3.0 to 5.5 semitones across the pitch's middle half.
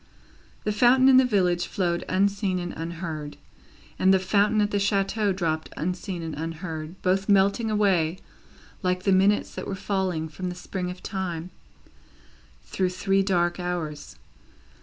No: narrow, 2.5 semitones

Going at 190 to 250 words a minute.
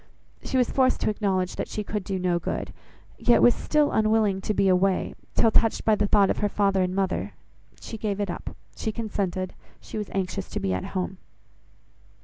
Yes: average, 200 wpm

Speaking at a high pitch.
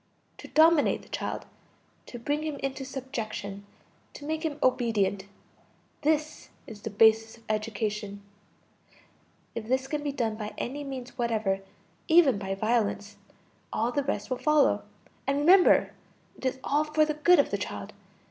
Yes: very high, 255 Hz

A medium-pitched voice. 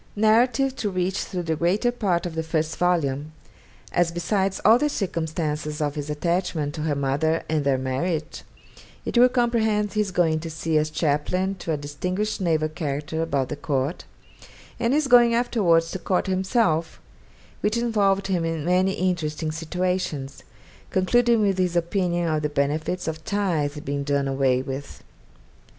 Yes: medium, 170 Hz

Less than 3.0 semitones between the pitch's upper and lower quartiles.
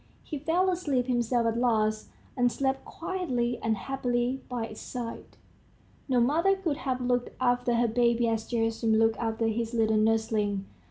Yes: narrow, 2.6 semitones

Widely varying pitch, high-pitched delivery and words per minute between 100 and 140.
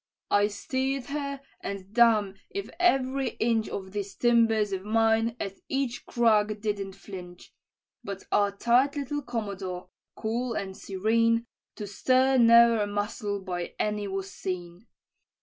No: average, 3.2 semitones; high, 215 Hz; slow, 135 wpm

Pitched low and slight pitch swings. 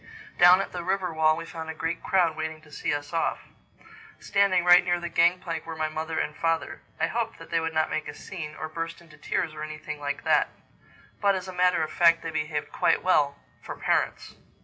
No: medium, 165 Hz; narrow, 2.1 semitones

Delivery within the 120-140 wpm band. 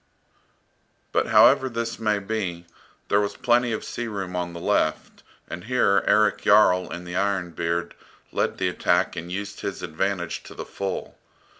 No: average, 165 wpm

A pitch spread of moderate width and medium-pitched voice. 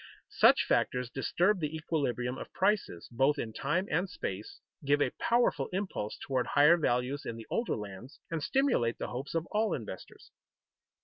No: wide, 6.9 semitones; medium, 145 Hz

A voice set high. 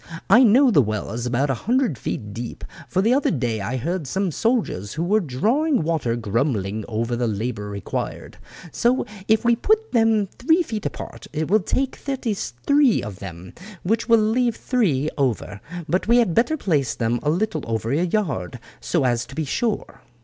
No: medium, 160 Hz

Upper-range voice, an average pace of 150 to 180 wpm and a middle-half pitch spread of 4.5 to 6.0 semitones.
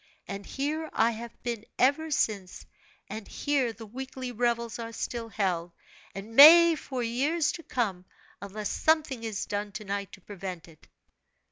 Yes: high, 230 Hz; average, 155 wpm; average, 4.8 semitones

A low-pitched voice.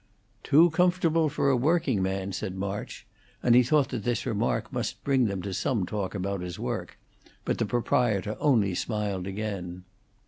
Yes: low, 105 Hz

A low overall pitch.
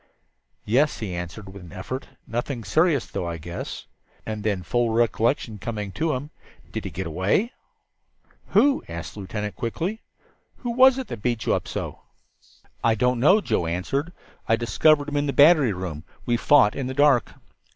Yes: low, 115 Hz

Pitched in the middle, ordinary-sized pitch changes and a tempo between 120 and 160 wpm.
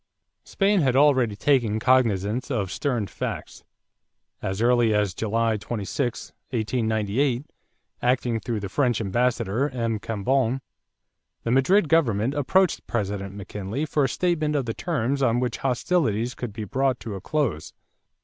No: low, 120 Hz; average, 4.2 semitones; average, 140 wpm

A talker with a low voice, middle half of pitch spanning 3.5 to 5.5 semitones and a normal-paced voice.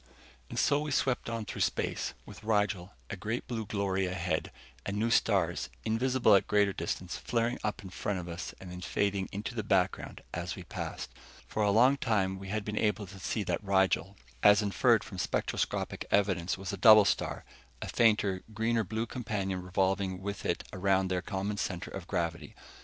No: low, 100 Hz; average, 2.7 semitones; average, 185 wpm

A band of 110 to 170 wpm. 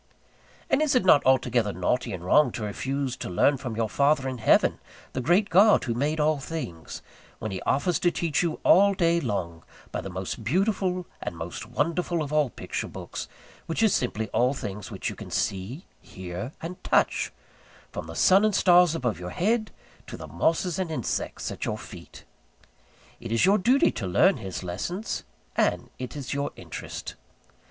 No: average, 185 wpm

